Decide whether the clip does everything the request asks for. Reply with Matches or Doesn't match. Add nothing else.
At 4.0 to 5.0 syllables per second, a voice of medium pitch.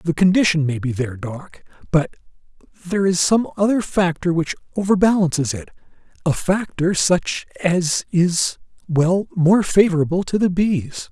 Matches